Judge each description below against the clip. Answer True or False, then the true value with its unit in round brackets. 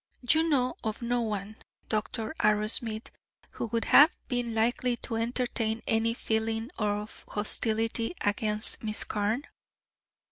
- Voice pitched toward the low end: False (225 Hz)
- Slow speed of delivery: True (120 wpm)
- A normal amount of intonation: False (1.8 semitones)